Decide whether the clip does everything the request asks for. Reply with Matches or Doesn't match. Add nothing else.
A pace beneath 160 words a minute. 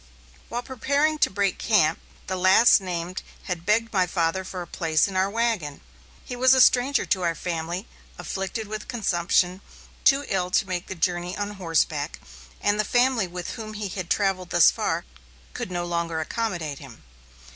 Doesn't match